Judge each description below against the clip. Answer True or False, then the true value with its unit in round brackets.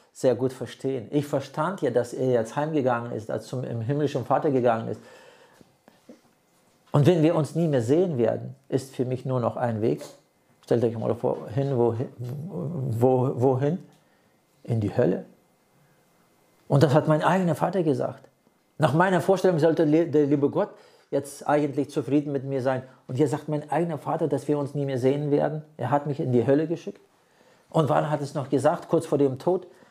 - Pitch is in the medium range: True (145 Hz)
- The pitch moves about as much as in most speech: True (3.0 semitones)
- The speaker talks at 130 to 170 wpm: False (185 wpm)